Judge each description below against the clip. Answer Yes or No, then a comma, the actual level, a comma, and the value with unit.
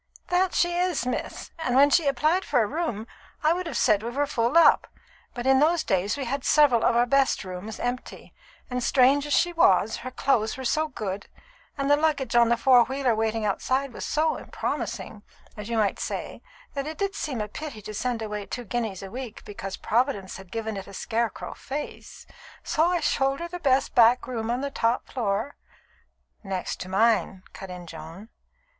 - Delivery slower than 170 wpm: No, average, 200 wpm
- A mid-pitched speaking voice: No, high, 245 Hz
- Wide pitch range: No, average, 4.9 semitones